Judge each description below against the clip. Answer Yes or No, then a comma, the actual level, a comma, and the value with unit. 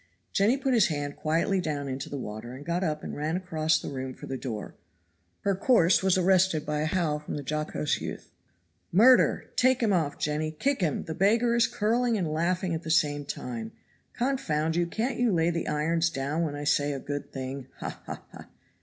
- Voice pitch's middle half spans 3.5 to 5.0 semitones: Yes, average, 4.6 semitones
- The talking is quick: Yes, fast, 210 wpm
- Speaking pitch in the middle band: Yes, medium, 160 Hz